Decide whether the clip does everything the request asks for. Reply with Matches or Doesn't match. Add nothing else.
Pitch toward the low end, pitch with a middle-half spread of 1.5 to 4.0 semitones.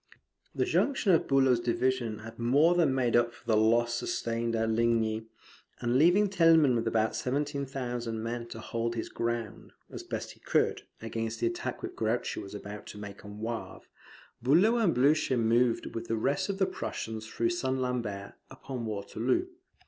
Matches